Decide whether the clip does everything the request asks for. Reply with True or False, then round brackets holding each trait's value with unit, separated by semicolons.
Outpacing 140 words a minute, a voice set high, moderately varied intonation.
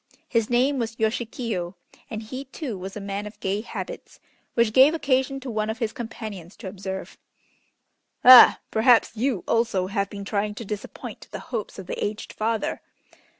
True (170 wpm; 220 Hz; 3.3 semitones)